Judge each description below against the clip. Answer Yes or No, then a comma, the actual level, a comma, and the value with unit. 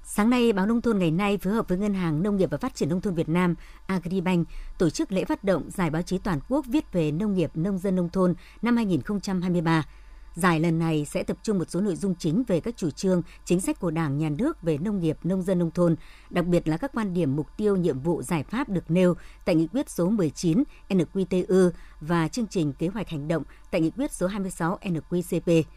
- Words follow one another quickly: No, average, 240 wpm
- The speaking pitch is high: No, medium, 180 Hz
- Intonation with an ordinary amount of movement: Yes, average, 3.1 semitones